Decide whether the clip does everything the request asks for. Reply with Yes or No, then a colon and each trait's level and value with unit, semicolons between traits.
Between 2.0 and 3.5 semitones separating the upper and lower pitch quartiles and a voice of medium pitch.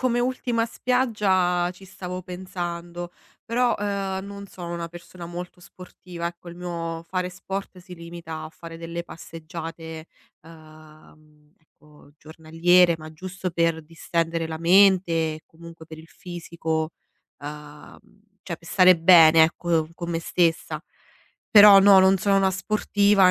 Yes: narrow, 2.4 semitones; medium, 170 Hz